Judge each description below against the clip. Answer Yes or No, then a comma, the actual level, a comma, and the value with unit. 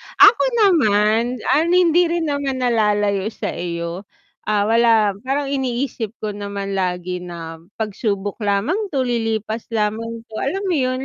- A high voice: Yes, high, 220 Hz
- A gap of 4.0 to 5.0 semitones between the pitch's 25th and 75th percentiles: Yes, average, 4.6 semitones